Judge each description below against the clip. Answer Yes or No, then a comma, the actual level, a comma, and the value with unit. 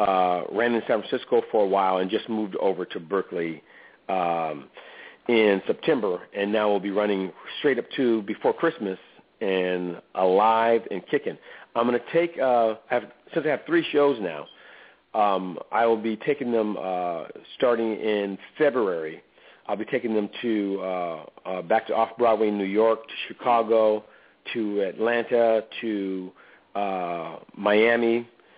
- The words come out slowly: No, average, 155 wpm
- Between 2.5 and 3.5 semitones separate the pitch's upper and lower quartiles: Yes, average, 3.0 semitones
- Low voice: Yes, low, 110 Hz